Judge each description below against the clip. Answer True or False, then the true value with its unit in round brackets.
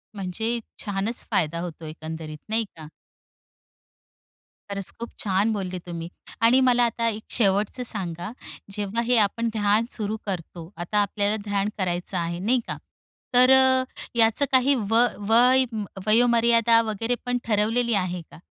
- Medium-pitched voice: False (210 Hz)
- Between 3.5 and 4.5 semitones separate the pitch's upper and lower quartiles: True (4.1 semitones)